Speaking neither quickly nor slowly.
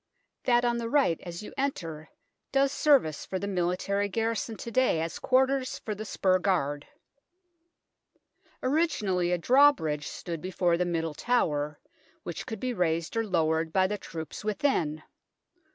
Yes: average, 150 wpm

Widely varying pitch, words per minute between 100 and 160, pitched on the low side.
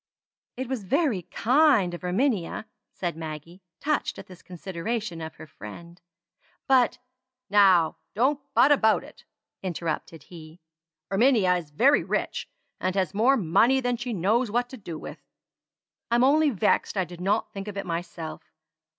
No: wide, 6.2 semitones; average, 150 wpm; high, 195 Hz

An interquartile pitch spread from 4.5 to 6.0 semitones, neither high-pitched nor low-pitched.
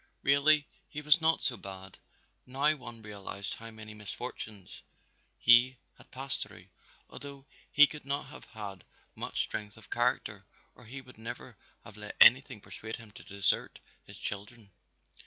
No: average, 4.8 semitones; low, 115 Hz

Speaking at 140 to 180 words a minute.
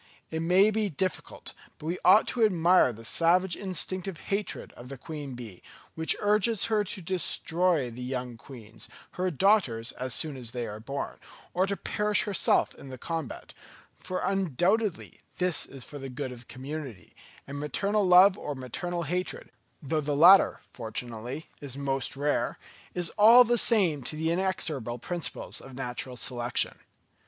Yes: average, 165 wpm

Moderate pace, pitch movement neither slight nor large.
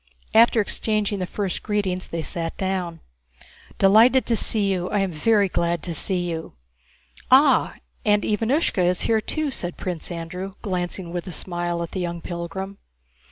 Yes: average, 165 wpm; average, 3.2 semitones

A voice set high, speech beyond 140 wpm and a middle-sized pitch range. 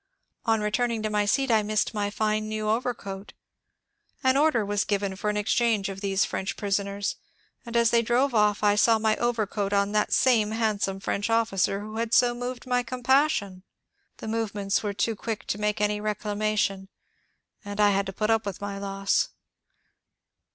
No: high, 210 Hz; average, 180 wpm; narrow, 2.1 semitones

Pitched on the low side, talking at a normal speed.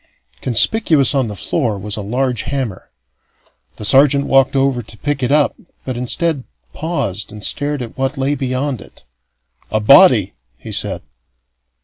Yes: low, 130 Hz; average, 150 wpm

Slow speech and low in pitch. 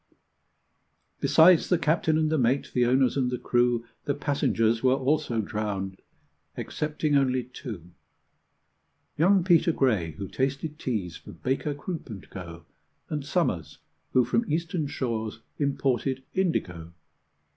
Yes: slow, 130 wpm; low, 130 Hz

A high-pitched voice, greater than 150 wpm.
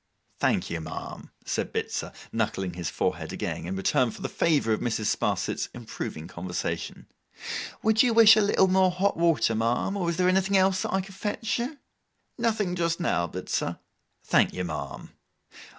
No: medium, 175 Hz; average, 170 wpm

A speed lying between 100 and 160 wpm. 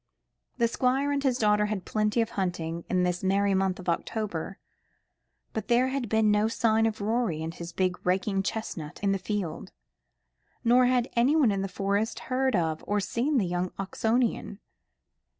No: average, 170 wpm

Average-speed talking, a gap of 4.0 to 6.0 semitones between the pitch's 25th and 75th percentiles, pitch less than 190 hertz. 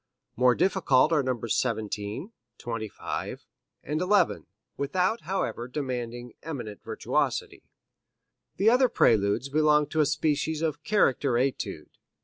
No: slow, 115 wpm; average, 5.0 semitones; medium, 140 Hz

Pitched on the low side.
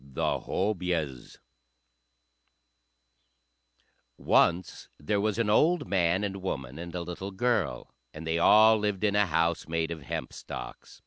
Yes: very low, 90 Hz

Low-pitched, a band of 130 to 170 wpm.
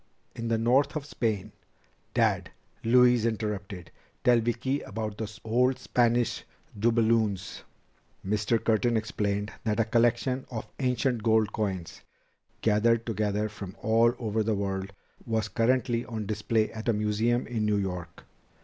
Yes: low, 110 Hz; average, 140 wpm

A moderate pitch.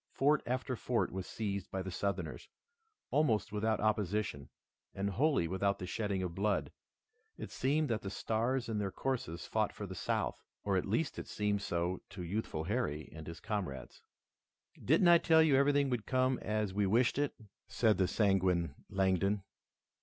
No: low, 105 Hz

